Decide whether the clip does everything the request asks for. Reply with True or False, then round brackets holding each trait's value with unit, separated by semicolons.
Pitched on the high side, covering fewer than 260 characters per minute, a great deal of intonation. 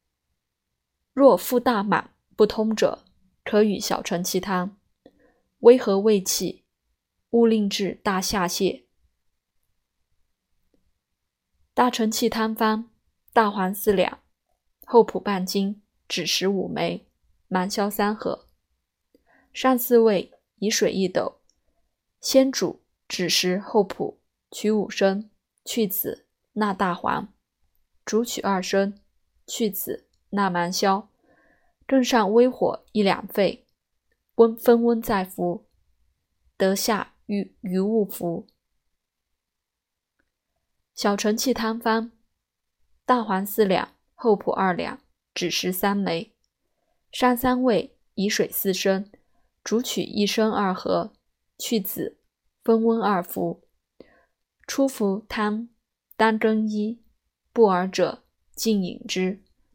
False (205 Hz; 140 characters per minute; 3.4 semitones)